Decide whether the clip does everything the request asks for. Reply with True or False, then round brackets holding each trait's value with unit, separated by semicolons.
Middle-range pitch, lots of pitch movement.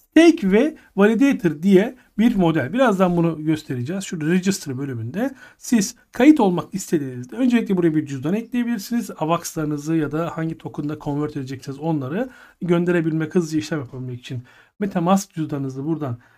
True (170 Hz; 5.8 semitones)